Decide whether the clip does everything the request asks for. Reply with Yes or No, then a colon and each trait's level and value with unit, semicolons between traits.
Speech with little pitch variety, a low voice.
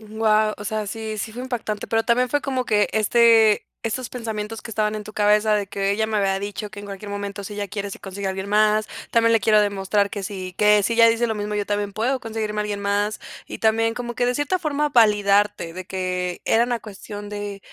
No: narrow, 1.8 semitones; high, 210 Hz